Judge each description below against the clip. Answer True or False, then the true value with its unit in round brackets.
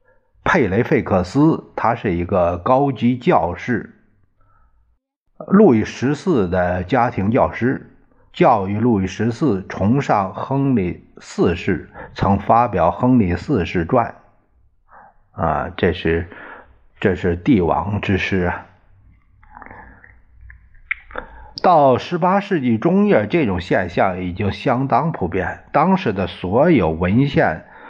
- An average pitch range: False (7.4 semitones)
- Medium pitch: False (115 Hz)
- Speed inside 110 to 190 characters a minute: True (165 characters per minute)